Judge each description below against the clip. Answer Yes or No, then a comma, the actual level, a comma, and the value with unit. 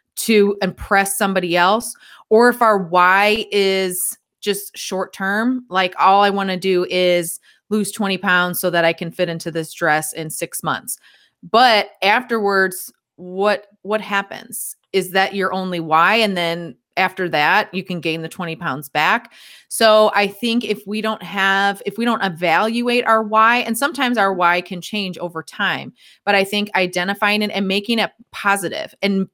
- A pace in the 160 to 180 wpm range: Yes, average, 175 wpm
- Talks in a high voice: Yes, high, 195 Hz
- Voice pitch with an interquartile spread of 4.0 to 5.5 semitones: No, average, 2.9 semitones